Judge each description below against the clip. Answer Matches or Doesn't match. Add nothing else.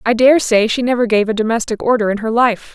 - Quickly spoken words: Matches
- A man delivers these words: Doesn't match